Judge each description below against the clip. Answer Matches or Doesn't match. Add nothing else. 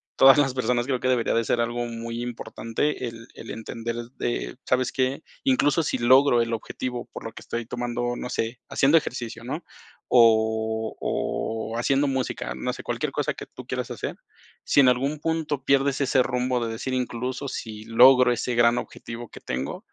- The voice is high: Doesn't match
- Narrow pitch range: Matches